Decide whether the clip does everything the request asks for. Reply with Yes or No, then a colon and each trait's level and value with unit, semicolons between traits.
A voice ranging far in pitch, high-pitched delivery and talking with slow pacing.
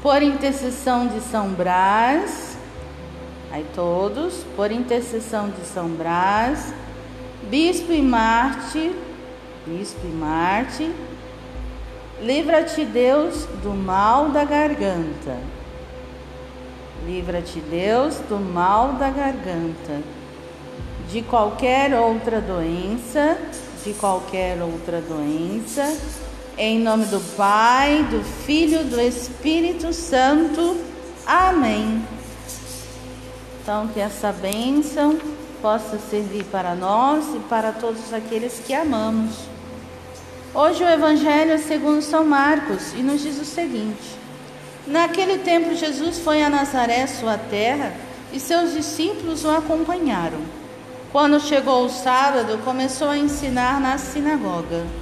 Yes: wide, 7.1 semitones; high, 245 Hz; slow, 105 wpm